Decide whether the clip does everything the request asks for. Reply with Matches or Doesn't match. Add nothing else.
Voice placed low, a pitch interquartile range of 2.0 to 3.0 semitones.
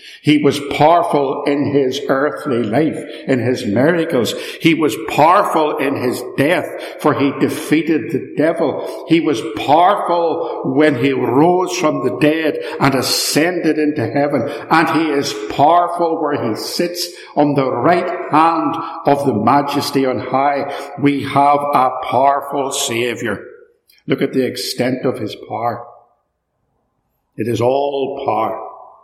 Doesn't match